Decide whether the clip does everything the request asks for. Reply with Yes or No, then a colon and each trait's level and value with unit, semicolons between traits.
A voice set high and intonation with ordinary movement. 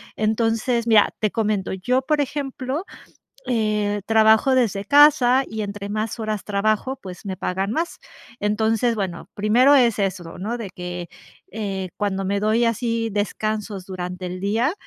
Yes: high, 215 Hz; average, 3.0 semitones